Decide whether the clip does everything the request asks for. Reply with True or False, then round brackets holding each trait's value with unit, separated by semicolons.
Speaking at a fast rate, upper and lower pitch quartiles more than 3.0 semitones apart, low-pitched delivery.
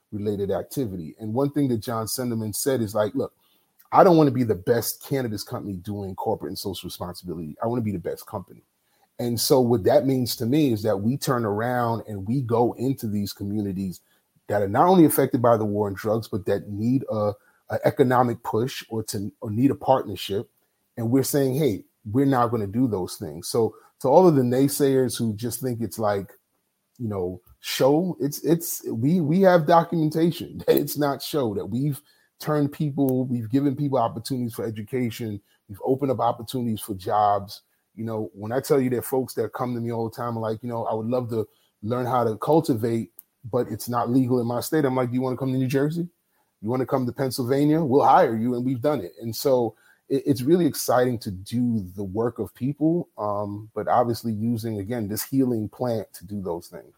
True (215 wpm; 3.9 semitones; 120 Hz)